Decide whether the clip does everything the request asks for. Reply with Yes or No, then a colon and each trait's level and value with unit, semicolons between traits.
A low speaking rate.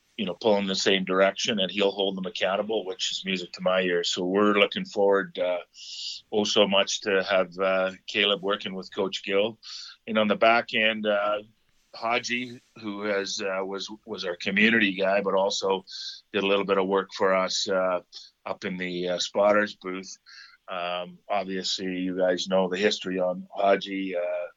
No: average, 185 wpm